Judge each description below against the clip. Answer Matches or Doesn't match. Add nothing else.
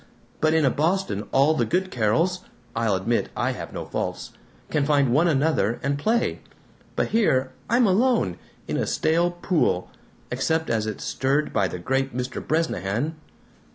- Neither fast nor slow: Matches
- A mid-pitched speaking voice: Matches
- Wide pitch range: Matches